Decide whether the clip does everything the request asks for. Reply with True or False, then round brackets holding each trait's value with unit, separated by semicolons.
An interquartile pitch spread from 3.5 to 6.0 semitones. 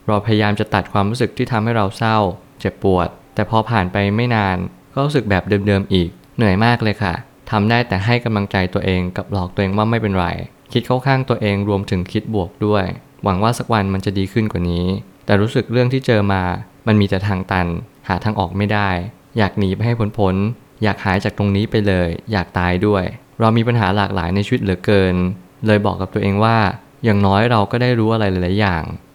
False (2.8 semitones)